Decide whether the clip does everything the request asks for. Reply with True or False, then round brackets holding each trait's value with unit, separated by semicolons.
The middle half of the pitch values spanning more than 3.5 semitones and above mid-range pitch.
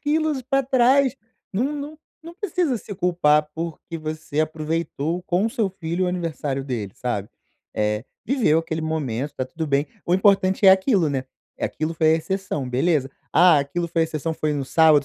False (5.0 semitones; 165 Hz)